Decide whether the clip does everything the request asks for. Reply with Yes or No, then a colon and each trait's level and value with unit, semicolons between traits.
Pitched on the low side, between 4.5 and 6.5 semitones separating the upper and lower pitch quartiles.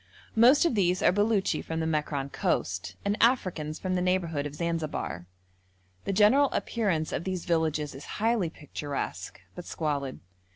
No: medium, 170 Hz; average, 5.1 semitones